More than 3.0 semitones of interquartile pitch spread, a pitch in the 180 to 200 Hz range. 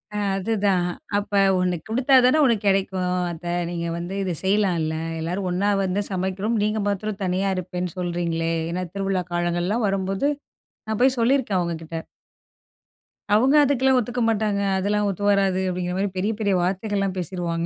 No: average, 2.7 semitones; high, 195 Hz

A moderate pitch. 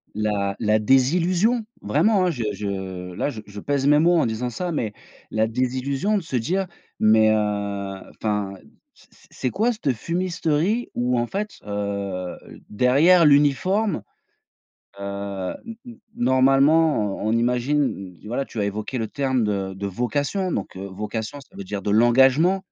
No: low, 125 Hz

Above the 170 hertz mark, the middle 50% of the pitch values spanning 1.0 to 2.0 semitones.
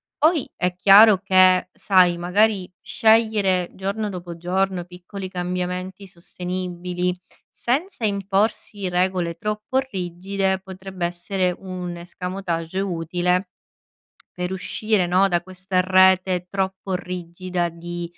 Yes: medium, 185 Hz; narrow, 1.6 semitones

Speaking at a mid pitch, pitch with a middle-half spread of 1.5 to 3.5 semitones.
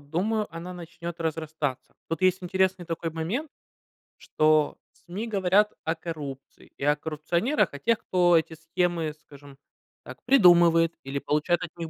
Yes: medium, 165 Hz; average, 2.8 semitones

